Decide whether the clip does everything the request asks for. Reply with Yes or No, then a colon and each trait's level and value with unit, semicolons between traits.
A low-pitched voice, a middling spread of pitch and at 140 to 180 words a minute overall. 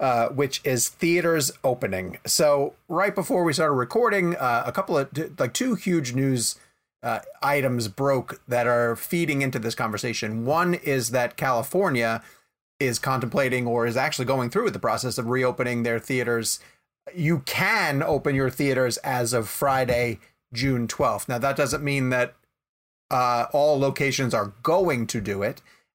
Yes: low, 130 Hz; average, 3.4 semitones; average, 160 wpm